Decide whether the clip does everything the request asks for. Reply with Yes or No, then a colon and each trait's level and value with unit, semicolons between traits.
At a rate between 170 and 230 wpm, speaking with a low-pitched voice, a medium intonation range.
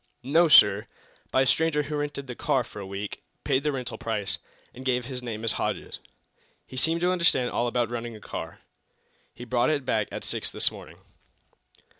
Yes: average, 195 wpm; low, 125 Hz; average, 4.2 semitones